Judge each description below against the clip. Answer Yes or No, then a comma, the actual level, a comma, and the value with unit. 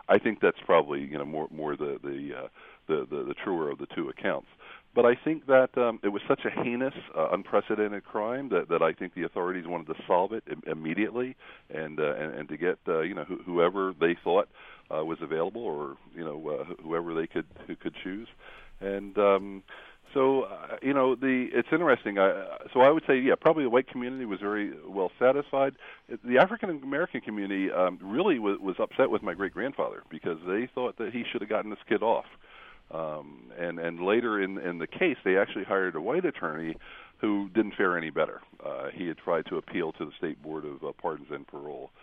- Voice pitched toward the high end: No, low, 105 Hz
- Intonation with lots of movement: Yes, wide, 6.4 semitones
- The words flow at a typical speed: No, fast, 215 wpm